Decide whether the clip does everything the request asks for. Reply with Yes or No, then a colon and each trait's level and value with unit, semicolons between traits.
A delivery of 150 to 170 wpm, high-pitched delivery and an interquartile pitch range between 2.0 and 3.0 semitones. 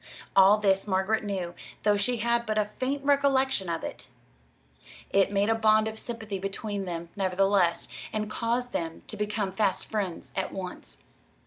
Yes: average, 160 wpm; high, 205 Hz; narrow, 2.5 semitones